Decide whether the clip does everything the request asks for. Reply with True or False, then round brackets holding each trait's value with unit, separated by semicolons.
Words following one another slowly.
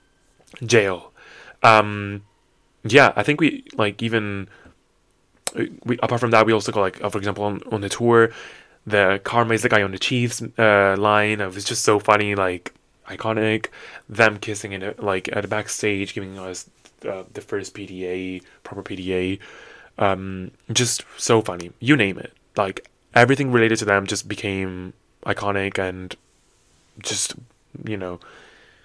False (155 wpm)